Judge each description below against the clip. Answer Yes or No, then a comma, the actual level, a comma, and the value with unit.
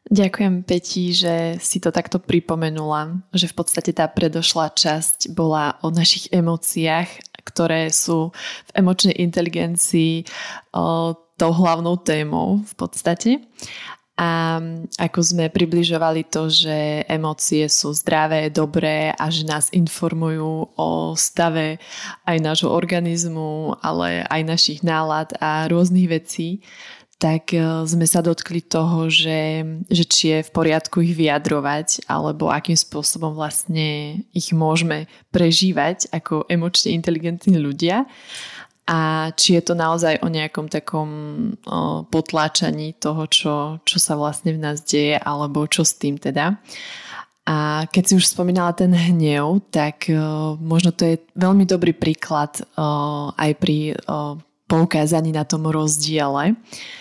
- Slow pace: No, average, 125 wpm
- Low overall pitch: No, medium, 165 Hz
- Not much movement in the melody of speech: Yes, narrow, 1.9 semitones